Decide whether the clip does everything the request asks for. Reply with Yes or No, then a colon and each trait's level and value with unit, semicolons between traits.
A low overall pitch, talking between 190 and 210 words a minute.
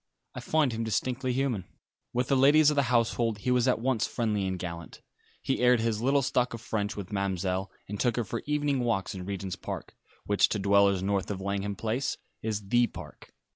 Yes: low, 110 Hz; fast, 205 wpm